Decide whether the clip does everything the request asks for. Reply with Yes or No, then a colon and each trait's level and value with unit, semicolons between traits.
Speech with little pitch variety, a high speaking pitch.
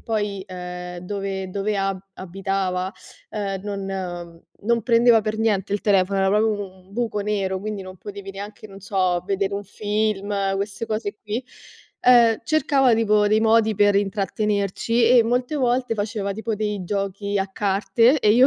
Yes: narrow, 2.1 semitones; high, 205 Hz